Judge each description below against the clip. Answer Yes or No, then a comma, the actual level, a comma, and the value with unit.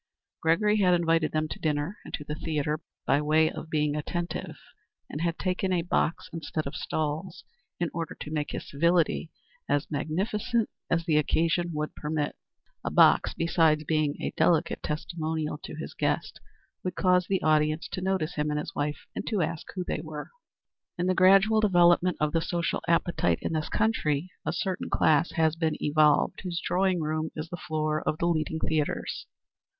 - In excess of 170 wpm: Yes, average, 180 wpm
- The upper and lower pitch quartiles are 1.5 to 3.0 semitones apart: Yes, narrow, 2.4 semitones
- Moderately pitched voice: Yes, medium, 160 Hz